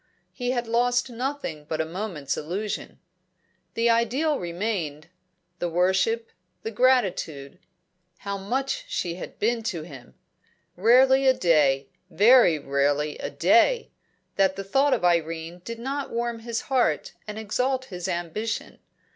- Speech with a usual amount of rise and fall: No, wide, 6.5 semitones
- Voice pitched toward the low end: No, high, 210 Hz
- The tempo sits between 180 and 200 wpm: No, slow, 135 wpm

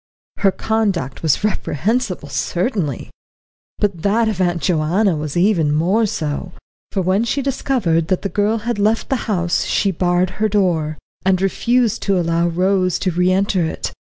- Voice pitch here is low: No, medium, 185 Hz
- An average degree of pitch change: Yes, average, 3.9 semitones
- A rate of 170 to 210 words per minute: No, average, 160 wpm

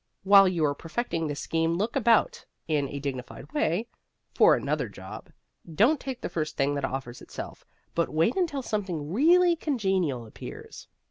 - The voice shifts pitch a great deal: Yes, wide, 8.5 semitones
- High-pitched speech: No, medium, 175 Hz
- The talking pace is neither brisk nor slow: Yes, average, 160 wpm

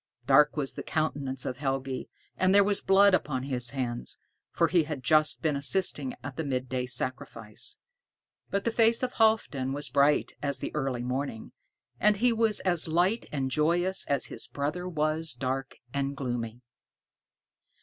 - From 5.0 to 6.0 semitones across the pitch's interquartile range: Yes, wide, 5.4 semitones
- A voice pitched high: No, medium, 145 Hz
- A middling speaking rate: Yes, average, 160 wpm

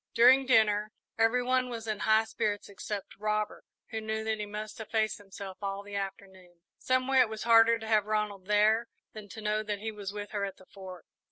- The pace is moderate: No, fast, 210 wpm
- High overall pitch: Yes, high, 215 Hz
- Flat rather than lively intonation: Yes, narrow, 1.6 semitones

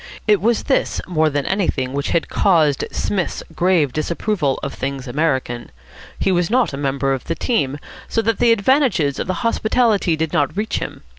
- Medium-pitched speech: Yes, medium, 165 Hz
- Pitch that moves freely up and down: Yes, wide, 7.0 semitones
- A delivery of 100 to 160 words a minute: No, average, 180 wpm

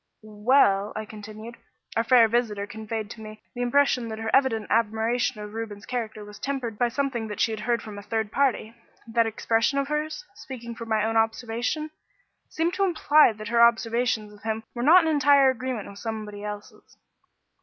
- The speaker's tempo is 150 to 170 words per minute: No, average, 185 wpm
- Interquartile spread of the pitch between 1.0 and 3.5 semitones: Yes, average, 2.9 semitones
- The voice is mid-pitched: No, high, 225 Hz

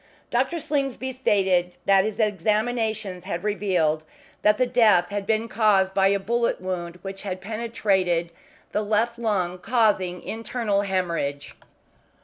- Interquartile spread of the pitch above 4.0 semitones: No, average, 3.5 semitones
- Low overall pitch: No, high, 205 Hz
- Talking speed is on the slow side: Yes, slow, 125 wpm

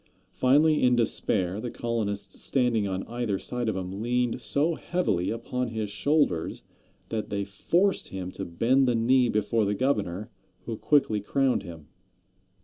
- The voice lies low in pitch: Yes, low, 115 Hz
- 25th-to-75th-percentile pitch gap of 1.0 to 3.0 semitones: No, average, 4.1 semitones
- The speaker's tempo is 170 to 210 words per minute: No, average, 150 wpm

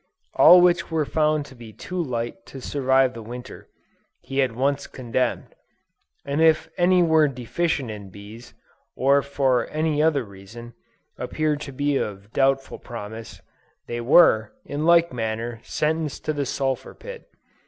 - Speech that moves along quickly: No, average, 150 wpm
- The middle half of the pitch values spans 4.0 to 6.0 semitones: Yes, average, 4.6 semitones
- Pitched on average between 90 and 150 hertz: Yes, low, 135 Hz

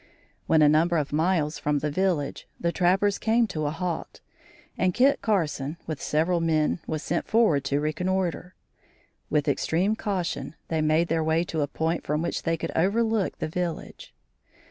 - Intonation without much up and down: No, average, 3.3 semitones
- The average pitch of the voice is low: No, medium, 165 Hz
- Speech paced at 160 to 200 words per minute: Yes, average, 170 wpm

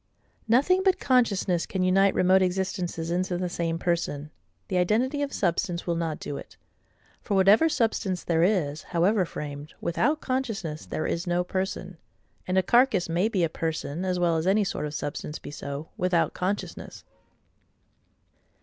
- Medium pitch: Yes, medium, 180 Hz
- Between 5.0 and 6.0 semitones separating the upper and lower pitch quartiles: No, average, 3.3 semitones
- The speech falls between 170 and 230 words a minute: No, average, 160 wpm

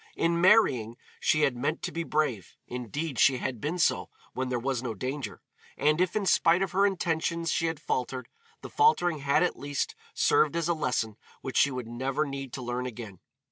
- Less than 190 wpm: No, average, 200 wpm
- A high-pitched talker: No, medium, 140 Hz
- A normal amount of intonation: Yes, average, 4.9 semitones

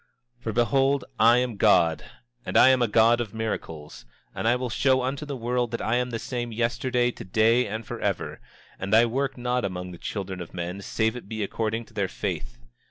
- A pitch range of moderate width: Yes, average, 3.2 semitones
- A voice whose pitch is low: Yes, low, 115 Hz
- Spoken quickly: Yes, fast, 210 wpm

